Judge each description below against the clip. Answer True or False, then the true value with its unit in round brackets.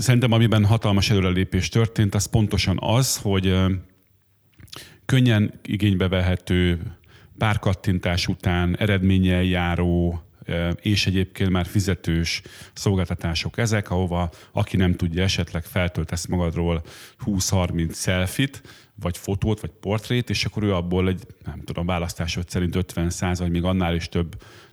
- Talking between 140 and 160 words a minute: False (125 wpm)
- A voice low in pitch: True (95 Hz)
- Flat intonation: False (3.1 semitones)